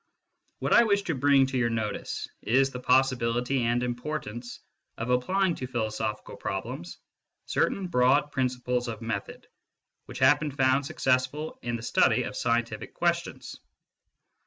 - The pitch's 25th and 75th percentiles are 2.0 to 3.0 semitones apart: Yes, narrow, 2.6 semitones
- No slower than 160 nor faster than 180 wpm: No, average, 140 wpm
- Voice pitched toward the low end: Yes, low, 125 Hz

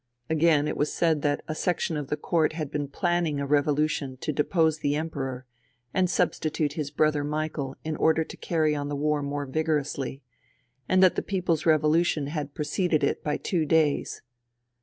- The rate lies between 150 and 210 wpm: Yes, average, 180 wpm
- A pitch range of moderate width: No, narrow, 1.9 semitones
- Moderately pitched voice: Yes, medium, 150 Hz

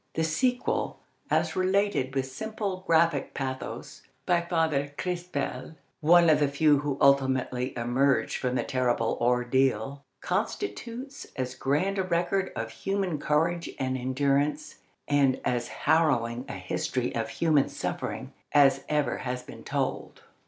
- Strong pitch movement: No, average, 4.7 semitones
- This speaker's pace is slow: Yes, slow, 130 wpm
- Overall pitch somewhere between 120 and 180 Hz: Yes, medium, 140 Hz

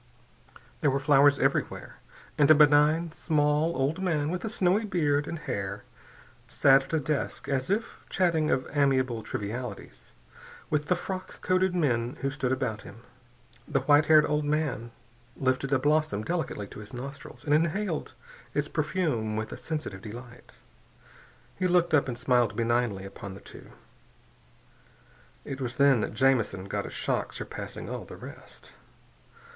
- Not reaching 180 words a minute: Yes, average, 155 wpm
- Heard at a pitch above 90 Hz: Yes, medium, 140 Hz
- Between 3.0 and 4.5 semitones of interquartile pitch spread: Yes, average, 4.2 semitones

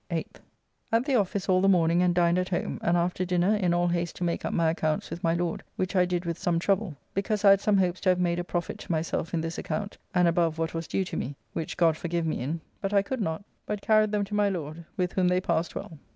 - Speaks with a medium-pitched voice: Yes, medium, 175 Hz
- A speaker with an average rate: No, fast, 270 wpm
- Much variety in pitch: No, narrow, 2.6 semitones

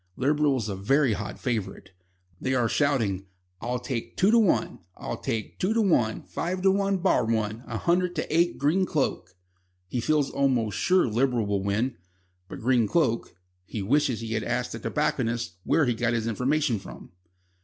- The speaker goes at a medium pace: Yes, average, 180 wpm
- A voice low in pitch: Yes, low, 125 Hz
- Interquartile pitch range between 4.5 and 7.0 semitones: Yes, average, 5.3 semitones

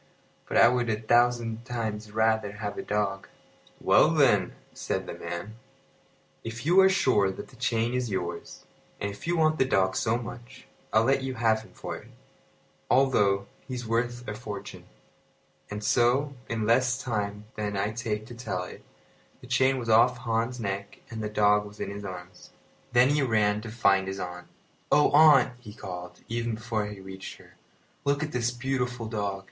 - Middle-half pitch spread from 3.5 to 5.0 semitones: No, average, 3.1 semitones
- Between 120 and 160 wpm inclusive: No, average, 180 wpm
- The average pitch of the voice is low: Yes, low, 115 Hz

